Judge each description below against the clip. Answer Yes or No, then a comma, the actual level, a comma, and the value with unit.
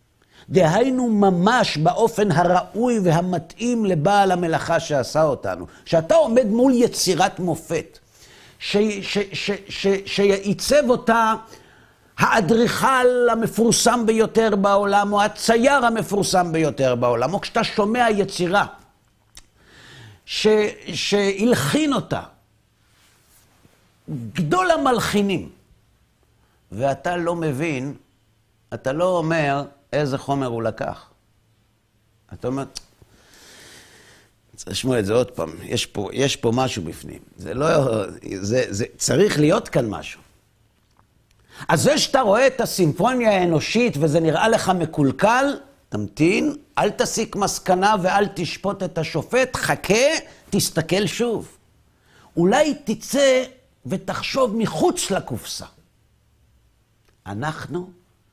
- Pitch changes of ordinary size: No, wide, 8.2 semitones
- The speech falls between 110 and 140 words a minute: No, slow, 100 wpm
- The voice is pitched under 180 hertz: No, medium, 185 Hz